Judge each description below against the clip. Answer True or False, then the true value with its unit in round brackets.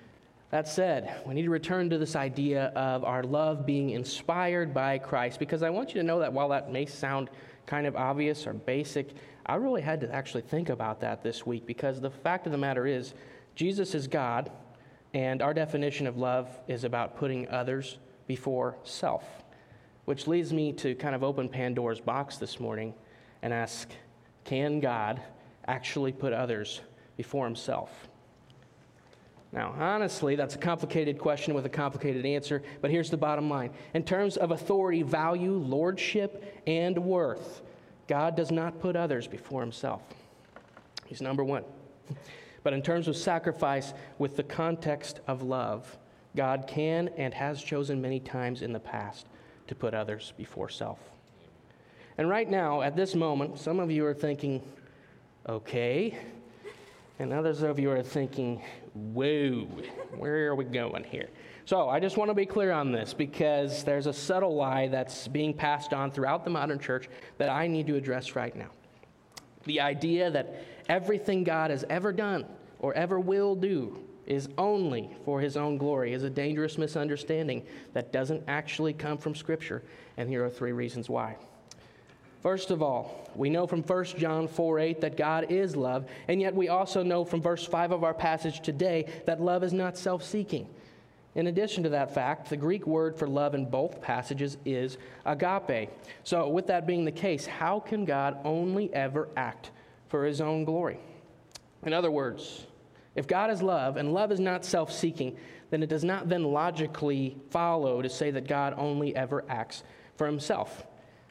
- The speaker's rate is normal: True (175 wpm)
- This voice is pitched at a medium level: True (145 Hz)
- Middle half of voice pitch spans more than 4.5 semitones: False (3.8 semitones)